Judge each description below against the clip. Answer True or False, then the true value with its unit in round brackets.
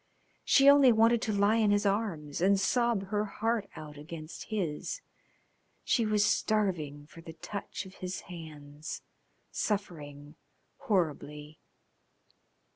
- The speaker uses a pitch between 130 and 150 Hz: False (195 Hz)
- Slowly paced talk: True (120 wpm)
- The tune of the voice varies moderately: False (5.7 semitones)